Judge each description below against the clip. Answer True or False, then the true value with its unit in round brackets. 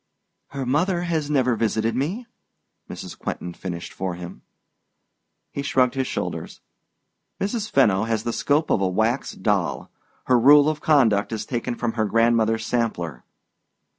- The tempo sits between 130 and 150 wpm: True (145 wpm)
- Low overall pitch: True (120 Hz)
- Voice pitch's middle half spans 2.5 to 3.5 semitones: False (4.8 semitones)